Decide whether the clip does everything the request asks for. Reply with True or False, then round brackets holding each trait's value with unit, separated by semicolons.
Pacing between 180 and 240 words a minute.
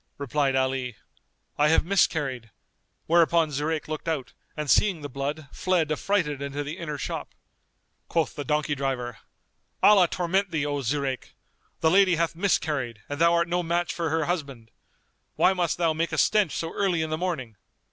False (170 wpm)